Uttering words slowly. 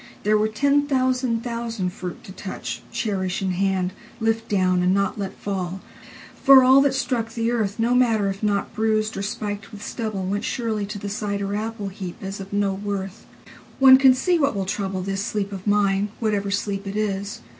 No: average, 165 wpm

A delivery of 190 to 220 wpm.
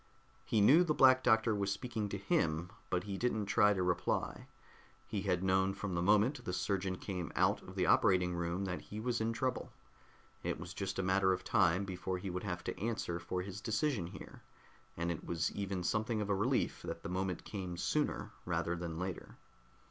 Yes: average, 200 wpm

